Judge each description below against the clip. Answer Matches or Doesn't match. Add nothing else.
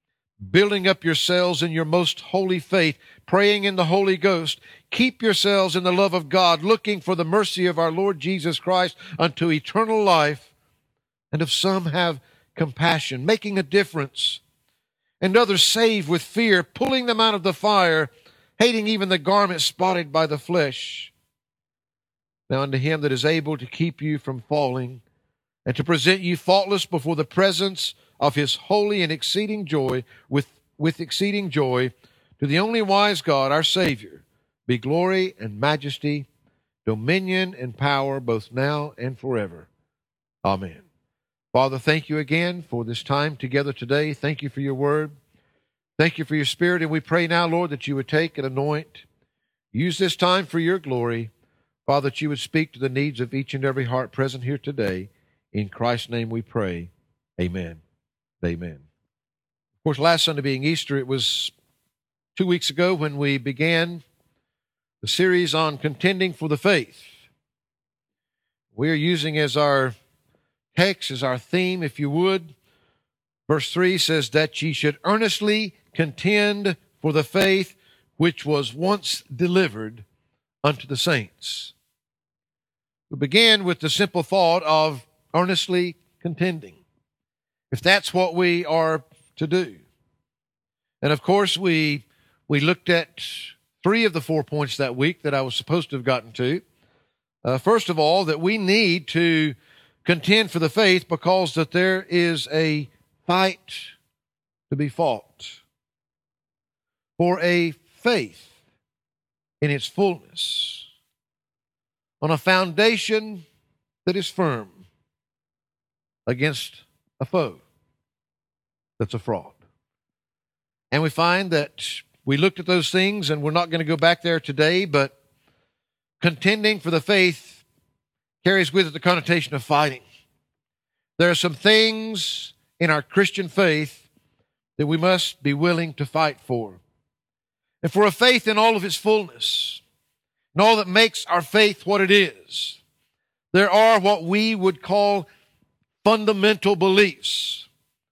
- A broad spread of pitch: Doesn't match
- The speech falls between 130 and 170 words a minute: Matches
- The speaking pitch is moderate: Matches